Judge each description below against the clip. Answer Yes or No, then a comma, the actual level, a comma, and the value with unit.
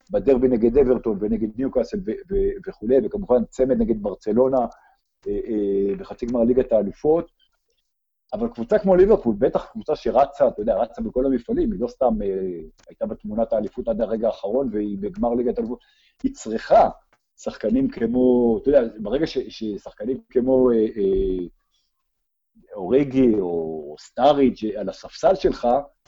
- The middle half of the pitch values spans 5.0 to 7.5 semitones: Yes, wide, 5.5 semitones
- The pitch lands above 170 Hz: No, low, 125 Hz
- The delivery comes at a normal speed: Yes, average, 130 wpm